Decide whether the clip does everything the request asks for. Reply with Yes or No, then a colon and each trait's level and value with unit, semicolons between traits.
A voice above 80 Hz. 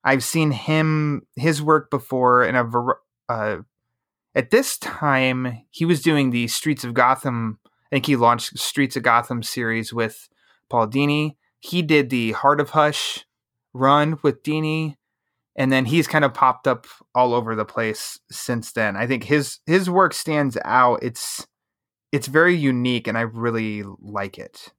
Yes: low, 135 Hz